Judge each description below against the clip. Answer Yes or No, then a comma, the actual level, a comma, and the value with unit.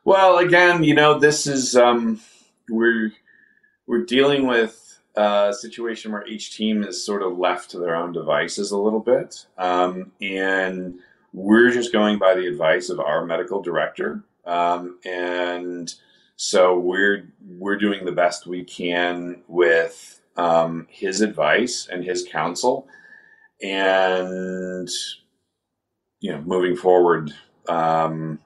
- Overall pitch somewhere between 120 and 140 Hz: No, very low, 95 Hz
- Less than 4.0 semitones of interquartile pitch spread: No, average, 4.7 semitones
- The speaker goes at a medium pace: No, slow, 130 wpm